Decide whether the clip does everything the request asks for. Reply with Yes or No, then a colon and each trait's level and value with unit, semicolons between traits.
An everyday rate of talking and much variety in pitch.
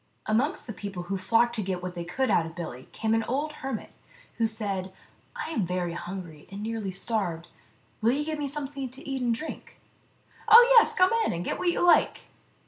No: fast, 220 wpm; wide, 6.9 semitones